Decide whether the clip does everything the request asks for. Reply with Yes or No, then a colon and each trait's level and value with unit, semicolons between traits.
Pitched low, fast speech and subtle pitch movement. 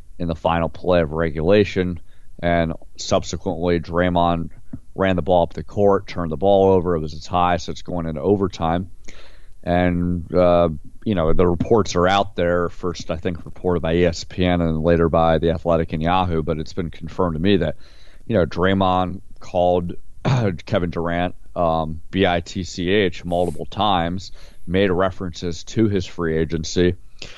No: very low, 90 Hz; average, 160 wpm; narrow, 2.0 semitones